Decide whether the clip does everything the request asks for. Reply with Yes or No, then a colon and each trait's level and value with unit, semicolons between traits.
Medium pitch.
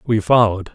No: low, 105 Hz